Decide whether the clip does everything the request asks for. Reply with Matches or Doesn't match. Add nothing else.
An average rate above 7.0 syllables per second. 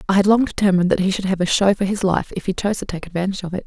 Matches